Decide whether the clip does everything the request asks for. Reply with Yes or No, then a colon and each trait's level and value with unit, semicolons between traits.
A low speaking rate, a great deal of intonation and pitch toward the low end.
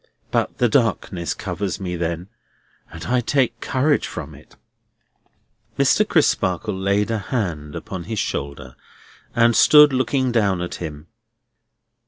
Yes: slow, 130 wpm; wide, 5.9 semitones; low, 100 Hz